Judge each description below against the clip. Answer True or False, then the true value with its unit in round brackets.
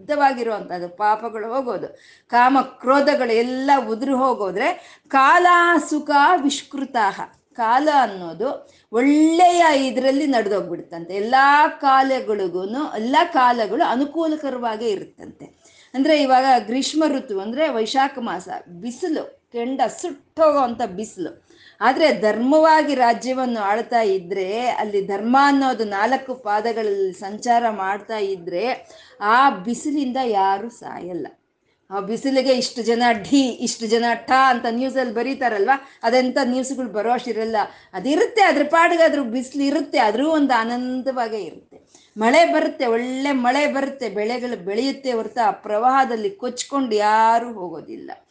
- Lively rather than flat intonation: False (4.1 semitones)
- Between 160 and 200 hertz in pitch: False (255 Hz)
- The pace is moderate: False (110 wpm)